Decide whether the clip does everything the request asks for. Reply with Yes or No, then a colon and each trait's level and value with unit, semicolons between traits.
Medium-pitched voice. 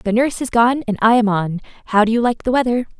No: high, 230 Hz